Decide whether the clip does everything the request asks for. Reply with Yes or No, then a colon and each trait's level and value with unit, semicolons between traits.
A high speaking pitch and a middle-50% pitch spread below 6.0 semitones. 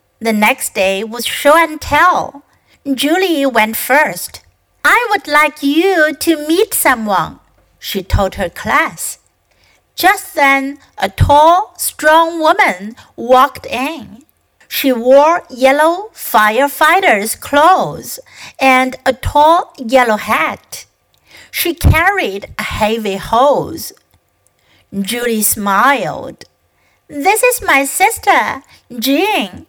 Yes: very high, 280 Hz; wide, 5.5 semitones